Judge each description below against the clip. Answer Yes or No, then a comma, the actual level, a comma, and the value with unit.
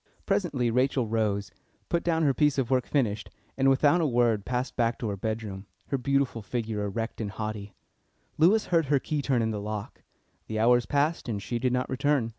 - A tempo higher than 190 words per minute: Yes, average, 200 wpm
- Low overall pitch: Yes, low, 120 Hz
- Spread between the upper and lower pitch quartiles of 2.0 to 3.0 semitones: No, average, 4.2 semitones